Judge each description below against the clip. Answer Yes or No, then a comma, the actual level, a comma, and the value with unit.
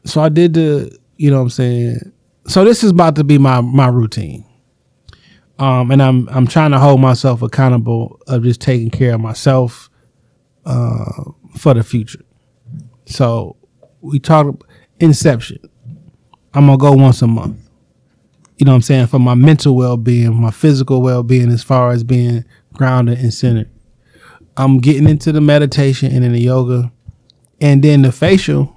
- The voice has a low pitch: Yes, low, 130 Hz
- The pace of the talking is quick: No, average, 165 wpm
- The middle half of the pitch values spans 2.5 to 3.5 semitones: Yes, average, 2.9 semitones